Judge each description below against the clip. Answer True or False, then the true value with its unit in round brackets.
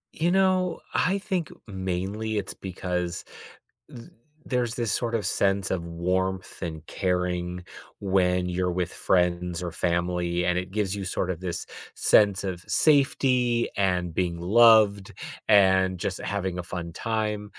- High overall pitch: False (95 Hz)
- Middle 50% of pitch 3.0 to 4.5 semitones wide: True (3.3 semitones)